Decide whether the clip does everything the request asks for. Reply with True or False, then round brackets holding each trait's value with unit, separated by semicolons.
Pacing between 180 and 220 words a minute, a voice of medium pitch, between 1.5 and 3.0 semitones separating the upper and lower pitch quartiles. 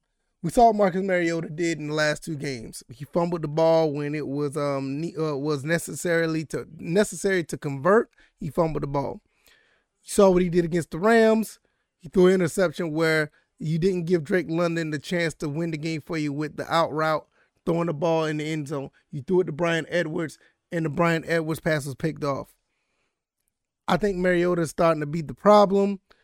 True (205 wpm; 165 Hz; 2.7 semitones)